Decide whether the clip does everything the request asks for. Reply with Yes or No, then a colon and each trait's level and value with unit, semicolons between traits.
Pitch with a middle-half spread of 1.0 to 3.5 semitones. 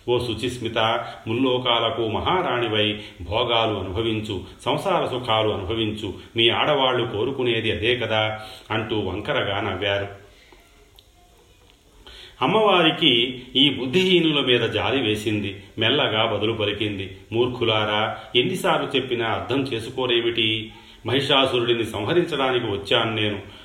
Yes: narrow, 2.6 semitones